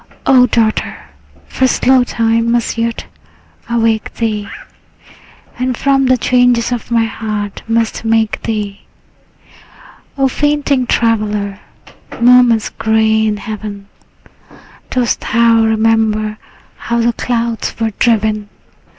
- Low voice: No, high, 225 Hz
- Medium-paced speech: No, slow, 110 wpm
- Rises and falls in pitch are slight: Yes, narrow, 1.9 semitones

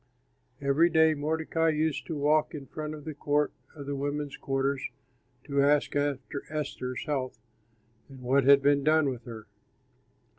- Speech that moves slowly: No, average, 155 wpm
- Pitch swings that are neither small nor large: No, narrow, 1.8 semitones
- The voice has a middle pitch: Yes, medium, 145 Hz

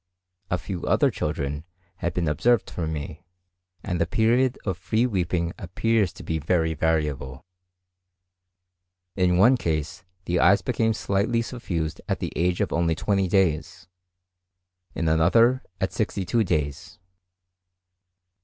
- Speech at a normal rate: No, slow, 130 wpm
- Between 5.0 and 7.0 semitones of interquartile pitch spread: No, average, 4.2 semitones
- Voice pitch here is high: No, very low, 90 Hz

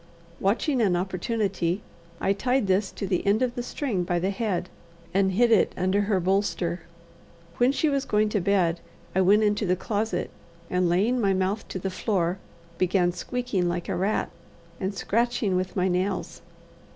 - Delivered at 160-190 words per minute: Yes, average, 175 wpm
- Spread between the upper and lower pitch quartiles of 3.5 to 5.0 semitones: No, average, 3.0 semitones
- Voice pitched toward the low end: No, high, 195 Hz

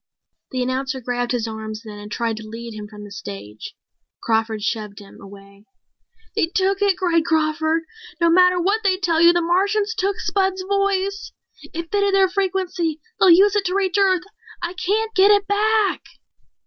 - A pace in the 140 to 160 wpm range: No, average, 175 wpm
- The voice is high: Yes, very high, 345 Hz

